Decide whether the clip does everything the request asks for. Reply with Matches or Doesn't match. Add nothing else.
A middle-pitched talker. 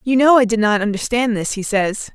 Doesn't match